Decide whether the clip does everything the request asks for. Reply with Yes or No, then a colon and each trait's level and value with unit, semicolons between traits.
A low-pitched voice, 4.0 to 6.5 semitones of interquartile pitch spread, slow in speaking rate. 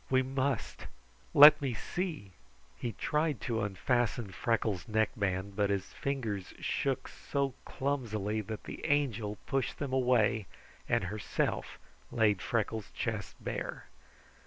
Yes: low, 115 Hz; average, 4.6 semitones; slow, 120 wpm